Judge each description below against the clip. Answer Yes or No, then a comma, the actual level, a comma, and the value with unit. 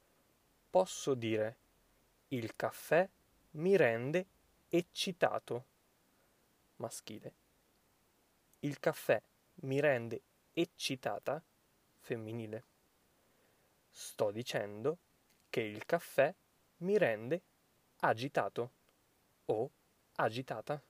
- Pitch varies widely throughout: Yes, wide, 6.6 semitones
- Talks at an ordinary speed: No, slow, 70 wpm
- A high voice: No, medium, 140 Hz